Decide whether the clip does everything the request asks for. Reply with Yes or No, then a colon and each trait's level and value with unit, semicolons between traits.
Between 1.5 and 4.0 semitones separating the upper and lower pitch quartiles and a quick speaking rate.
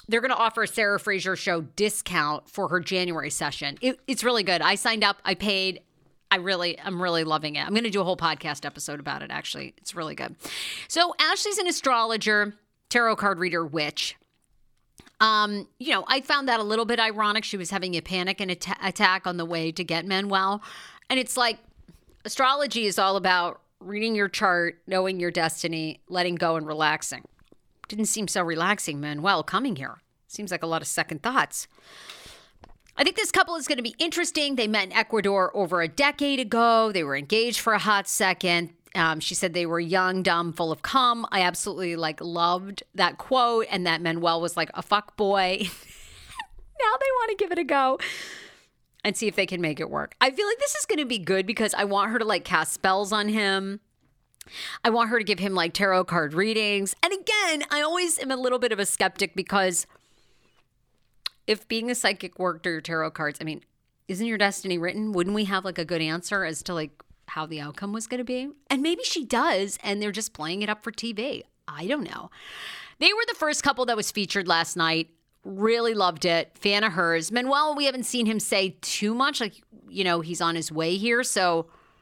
No: average, 5.0 semitones; fast, 210 wpm